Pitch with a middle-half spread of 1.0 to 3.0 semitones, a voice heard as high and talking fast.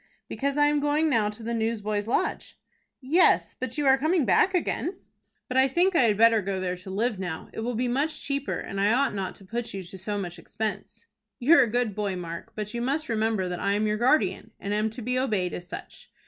No: average, 4.9 semitones; high, 225 Hz; fast, 235 wpm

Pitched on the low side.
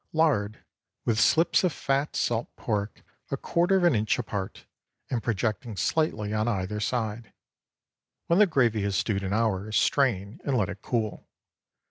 Yes: low, 110 Hz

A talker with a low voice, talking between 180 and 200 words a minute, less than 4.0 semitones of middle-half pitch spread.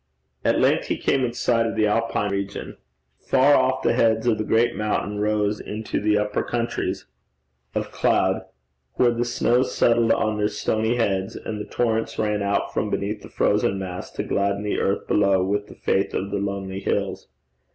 Yes: low, 105 Hz; average, 185 wpm; narrow, 2.5 semitones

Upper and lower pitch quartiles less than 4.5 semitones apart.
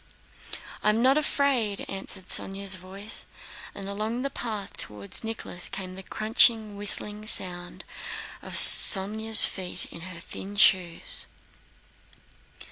Yes: narrow, 2.6 semitones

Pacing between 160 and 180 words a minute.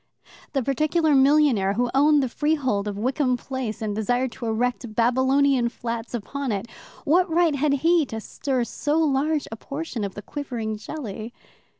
Yes: average, 165 wpm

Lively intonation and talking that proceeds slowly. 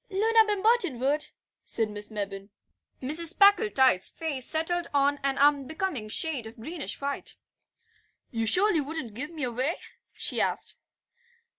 Yes: wide, 5.9 semitones; slow, 130 wpm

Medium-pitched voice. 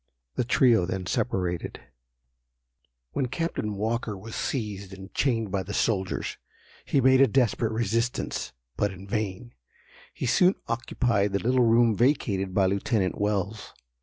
No: low, 110 Hz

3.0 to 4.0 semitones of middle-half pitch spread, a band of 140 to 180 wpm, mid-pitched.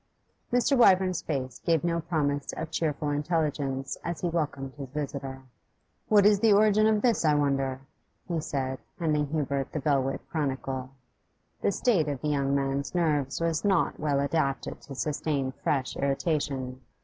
Yes: average, 3.6 semitones; average, 155 wpm; medium, 145 Hz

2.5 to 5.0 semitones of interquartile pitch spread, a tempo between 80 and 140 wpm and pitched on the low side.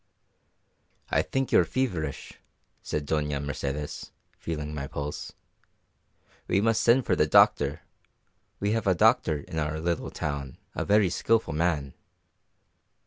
No: wide, 5.6 semitones; slow, 135 wpm; very low, 80 Hz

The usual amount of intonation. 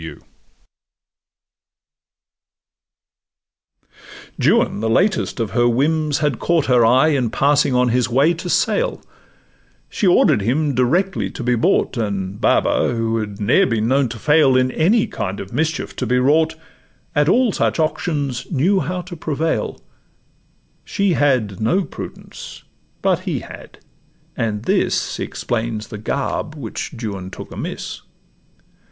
No: wide, 5.7 semitones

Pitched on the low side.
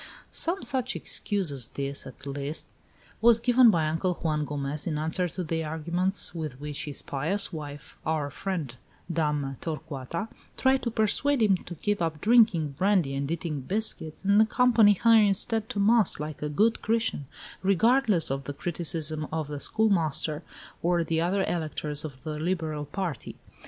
No: medium, 165 Hz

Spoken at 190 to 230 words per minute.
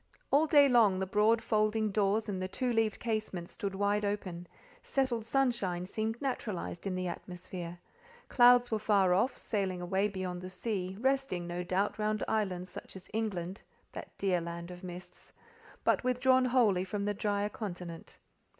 No: average, 155 wpm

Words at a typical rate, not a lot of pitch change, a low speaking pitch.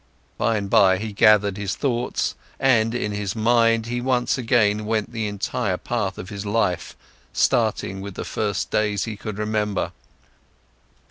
Yes: average, 155 wpm; narrow, 2.1 semitones; low, 105 Hz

